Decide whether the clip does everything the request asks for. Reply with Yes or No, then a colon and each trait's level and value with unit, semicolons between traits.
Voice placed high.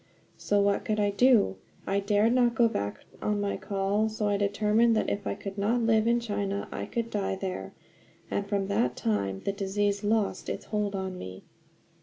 Yes: high, 205 Hz